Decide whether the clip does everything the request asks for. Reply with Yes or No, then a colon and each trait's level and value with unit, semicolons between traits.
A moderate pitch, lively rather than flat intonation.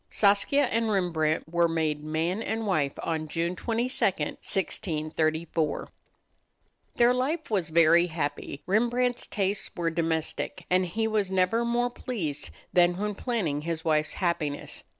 Yes: medium, 175 Hz; wide, 5.7 semitones